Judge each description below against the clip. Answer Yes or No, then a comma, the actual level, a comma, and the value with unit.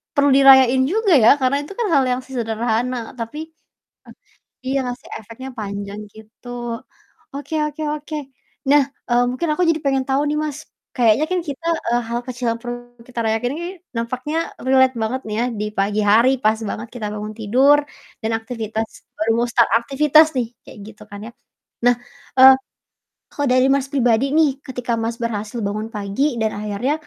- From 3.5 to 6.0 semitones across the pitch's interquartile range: Yes, average, 3.8 semitones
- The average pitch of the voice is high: Yes, high, 245 Hz